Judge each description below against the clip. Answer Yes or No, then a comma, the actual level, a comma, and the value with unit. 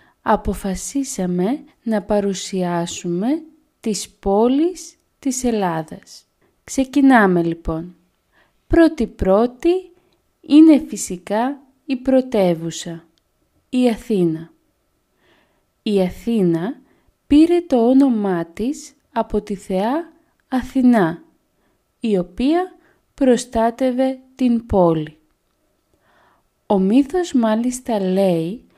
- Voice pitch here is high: Yes, high, 235 Hz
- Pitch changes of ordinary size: No, wide, 6.4 semitones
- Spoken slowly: Yes, slow, 75 wpm